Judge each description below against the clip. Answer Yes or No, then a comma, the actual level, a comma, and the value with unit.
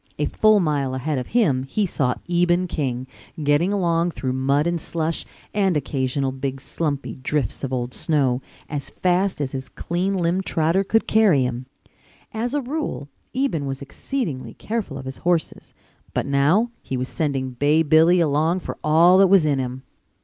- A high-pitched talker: No, medium, 155 Hz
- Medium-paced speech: Yes, average, 170 wpm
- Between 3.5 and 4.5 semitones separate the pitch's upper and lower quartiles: No, average, 5.2 semitones